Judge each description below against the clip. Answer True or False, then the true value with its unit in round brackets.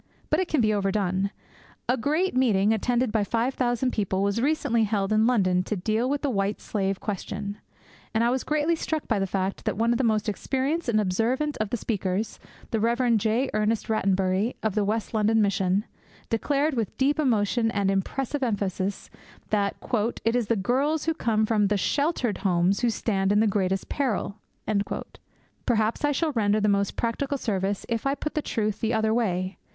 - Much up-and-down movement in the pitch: False (3.8 semitones)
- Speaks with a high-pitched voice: True (220 Hz)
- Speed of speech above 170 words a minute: True (190 wpm)